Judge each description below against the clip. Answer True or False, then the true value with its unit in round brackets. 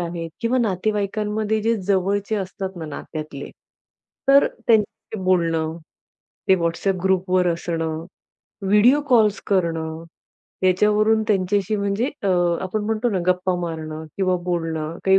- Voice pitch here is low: False (190 Hz)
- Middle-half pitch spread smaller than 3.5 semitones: False (3.9 semitones)